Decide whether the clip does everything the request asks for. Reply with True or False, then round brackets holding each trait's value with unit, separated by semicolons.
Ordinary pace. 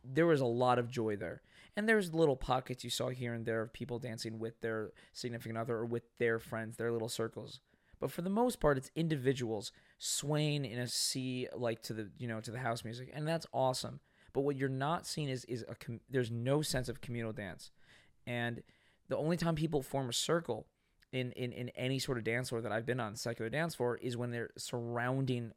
False (220 wpm)